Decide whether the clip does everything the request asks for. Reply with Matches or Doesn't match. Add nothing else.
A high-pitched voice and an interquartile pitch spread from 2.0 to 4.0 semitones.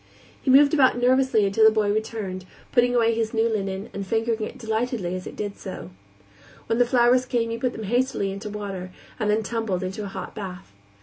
Matches